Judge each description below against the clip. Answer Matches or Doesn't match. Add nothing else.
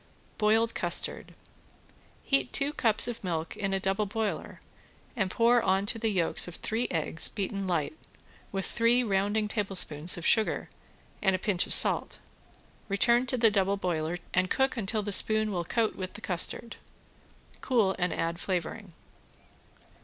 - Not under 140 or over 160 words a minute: Matches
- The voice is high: Matches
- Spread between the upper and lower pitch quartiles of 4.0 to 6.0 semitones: Doesn't match